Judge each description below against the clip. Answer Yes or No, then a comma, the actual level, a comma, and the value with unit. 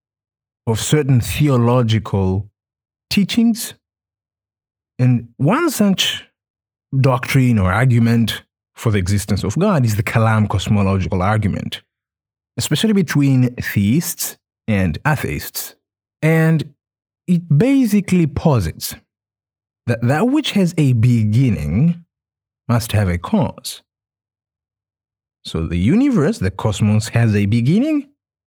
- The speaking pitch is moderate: No, low, 115 Hz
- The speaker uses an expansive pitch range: Yes, wide, 5.9 semitones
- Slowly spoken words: Yes, slow, 100 wpm